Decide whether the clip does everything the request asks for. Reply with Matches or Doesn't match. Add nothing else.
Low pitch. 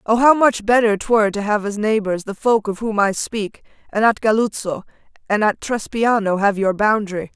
Doesn't match